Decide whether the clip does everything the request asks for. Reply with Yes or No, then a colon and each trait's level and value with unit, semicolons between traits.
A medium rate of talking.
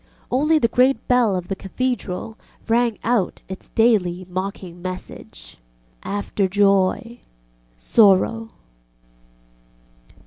No: slow, 95 wpm